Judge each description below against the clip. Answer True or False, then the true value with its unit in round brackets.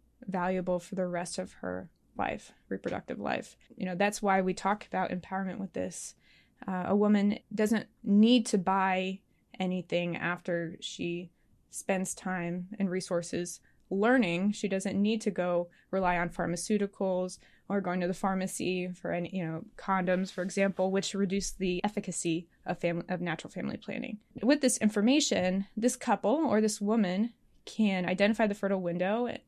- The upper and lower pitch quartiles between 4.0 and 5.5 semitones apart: False (2.5 semitones)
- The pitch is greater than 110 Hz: True (190 Hz)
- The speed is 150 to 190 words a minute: True (155 wpm)